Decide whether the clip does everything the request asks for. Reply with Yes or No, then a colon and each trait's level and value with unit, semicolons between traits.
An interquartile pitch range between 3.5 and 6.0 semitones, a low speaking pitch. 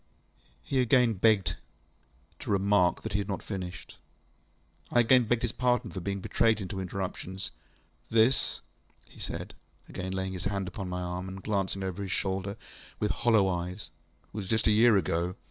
No: average, 3.1 semitones; very low, 95 Hz